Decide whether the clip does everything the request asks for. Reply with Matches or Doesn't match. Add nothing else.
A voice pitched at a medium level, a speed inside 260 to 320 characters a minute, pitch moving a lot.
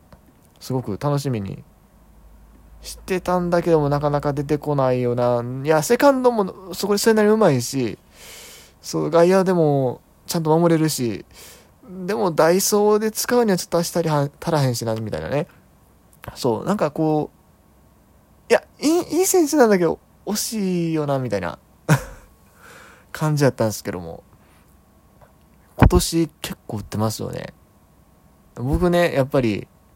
Matches